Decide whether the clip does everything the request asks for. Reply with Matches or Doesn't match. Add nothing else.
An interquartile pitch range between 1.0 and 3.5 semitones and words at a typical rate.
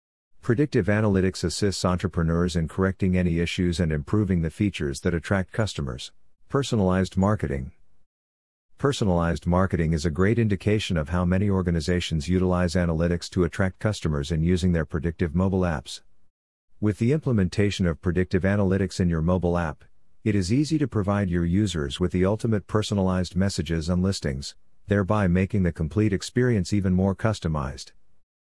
Matches